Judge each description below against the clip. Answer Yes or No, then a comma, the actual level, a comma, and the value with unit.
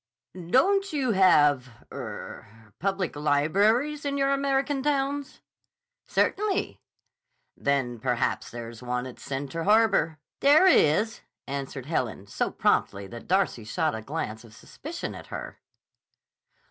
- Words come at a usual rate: No, slow, 115 wpm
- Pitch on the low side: No, medium, 165 Hz